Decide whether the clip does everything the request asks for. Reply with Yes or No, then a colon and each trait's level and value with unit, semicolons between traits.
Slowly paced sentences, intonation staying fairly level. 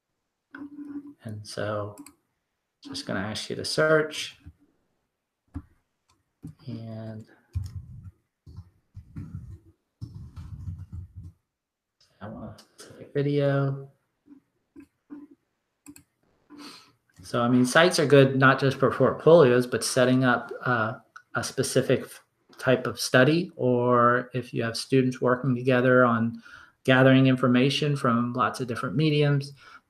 No: slow, 100 wpm; average, 3.9 semitones